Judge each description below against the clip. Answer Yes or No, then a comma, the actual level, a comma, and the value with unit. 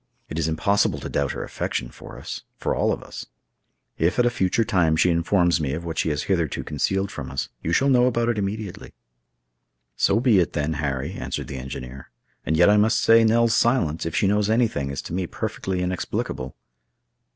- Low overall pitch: Yes, very low, 90 Hz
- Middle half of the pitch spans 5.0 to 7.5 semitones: Yes, wide, 5.6 semitones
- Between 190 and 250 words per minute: Yes, average, 200 wpm